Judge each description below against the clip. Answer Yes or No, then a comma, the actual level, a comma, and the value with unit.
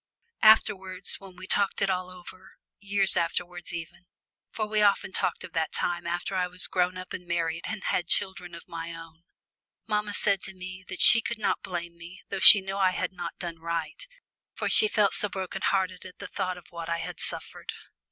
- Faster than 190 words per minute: Yes, fast, 205 wpm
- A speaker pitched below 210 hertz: Yes, medium, 185 Hz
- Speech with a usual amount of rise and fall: No, narrow, 2.2 semitones